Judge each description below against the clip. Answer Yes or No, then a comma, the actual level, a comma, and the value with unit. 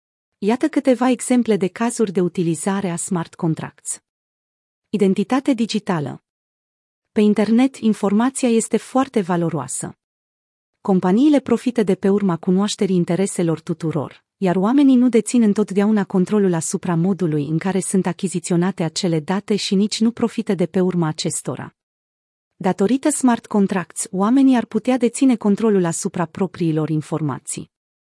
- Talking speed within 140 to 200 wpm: No, average, 125 wpm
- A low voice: No, high, 195 Hz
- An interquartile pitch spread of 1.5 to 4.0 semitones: No, average, 4.7 semitones